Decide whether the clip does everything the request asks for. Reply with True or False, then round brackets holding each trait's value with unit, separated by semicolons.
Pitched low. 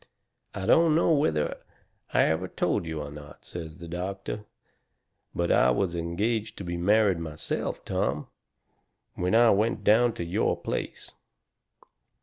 True (90 Hz)